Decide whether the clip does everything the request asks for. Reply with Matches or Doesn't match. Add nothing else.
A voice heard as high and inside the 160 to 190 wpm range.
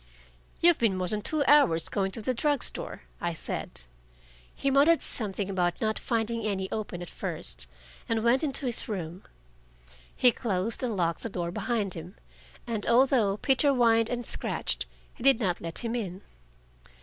Matches